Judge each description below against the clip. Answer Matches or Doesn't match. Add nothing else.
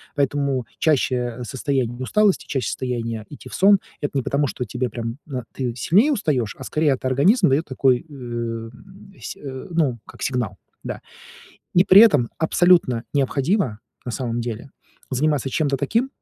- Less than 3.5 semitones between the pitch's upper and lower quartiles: Doesn't match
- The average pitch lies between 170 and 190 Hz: Doesn't match